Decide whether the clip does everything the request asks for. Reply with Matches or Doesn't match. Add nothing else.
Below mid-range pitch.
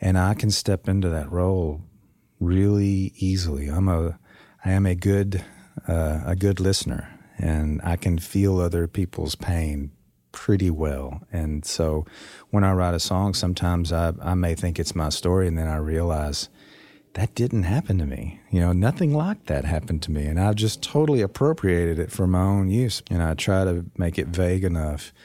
Matches